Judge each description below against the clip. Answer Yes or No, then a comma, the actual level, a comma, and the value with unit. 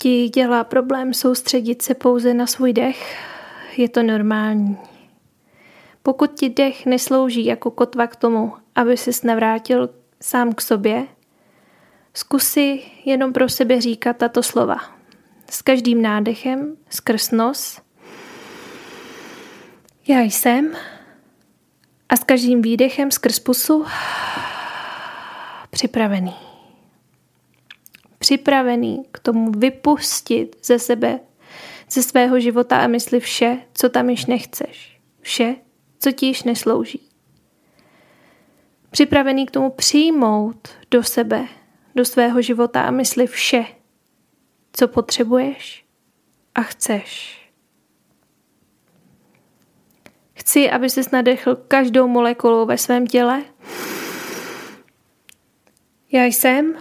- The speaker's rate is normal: No, slow, 100 wpm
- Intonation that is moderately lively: No, narrow, 2.1 semitones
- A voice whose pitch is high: Yes, very high, 250 Hz